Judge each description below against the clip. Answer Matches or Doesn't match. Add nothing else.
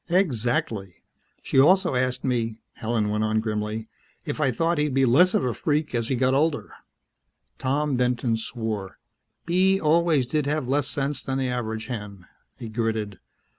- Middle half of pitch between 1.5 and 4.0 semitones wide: Doesn't match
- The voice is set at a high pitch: Doesn't match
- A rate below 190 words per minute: Matches